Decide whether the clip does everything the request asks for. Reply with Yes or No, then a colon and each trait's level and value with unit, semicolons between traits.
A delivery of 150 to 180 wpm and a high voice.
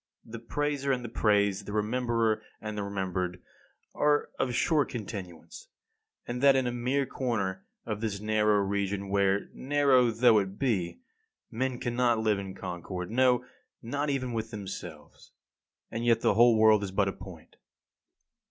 No: average, 155 wpm; low, 110 Hz